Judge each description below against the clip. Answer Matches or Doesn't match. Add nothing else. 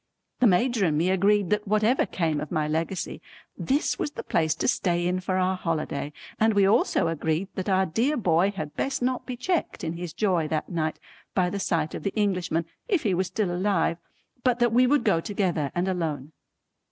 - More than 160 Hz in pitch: Matches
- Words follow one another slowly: Doesn't match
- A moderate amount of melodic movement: Matches